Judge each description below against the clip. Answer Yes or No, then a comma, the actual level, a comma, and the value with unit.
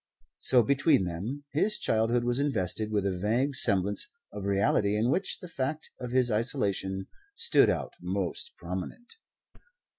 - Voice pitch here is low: Yes, low, 110 Hz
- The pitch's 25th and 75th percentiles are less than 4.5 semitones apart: No, wide, 5.6 semitones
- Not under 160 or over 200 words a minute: No, average, 145 wpm